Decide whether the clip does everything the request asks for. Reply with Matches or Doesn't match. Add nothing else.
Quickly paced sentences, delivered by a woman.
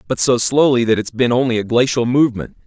Doesn't match